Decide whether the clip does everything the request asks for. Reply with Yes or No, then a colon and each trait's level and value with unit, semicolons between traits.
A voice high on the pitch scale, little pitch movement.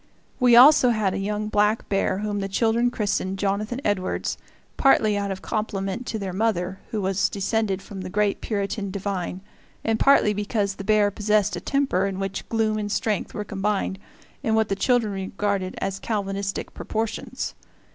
Yes: high, 205 Hz; narrow, 2.0 semitones